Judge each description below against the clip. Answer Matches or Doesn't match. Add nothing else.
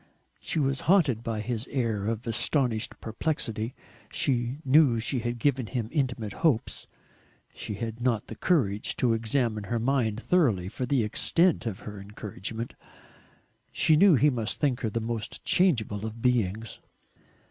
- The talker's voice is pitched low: Matches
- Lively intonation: Doesn't match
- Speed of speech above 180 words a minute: Doesn't match